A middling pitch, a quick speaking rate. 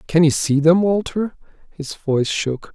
No: medium, 160 Hz; average, 175 wpm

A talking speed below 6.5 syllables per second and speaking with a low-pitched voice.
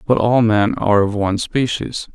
Yes: 5.0 syllables/s; low, 110 Hz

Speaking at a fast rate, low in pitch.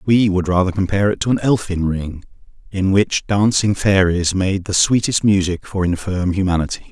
No: average, 175 wpm; very low, 95 Hz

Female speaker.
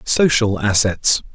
No: male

